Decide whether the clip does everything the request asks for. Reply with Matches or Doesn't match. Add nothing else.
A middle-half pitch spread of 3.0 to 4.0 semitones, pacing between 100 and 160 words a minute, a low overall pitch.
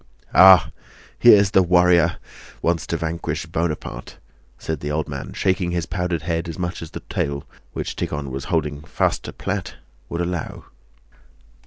Doesn't match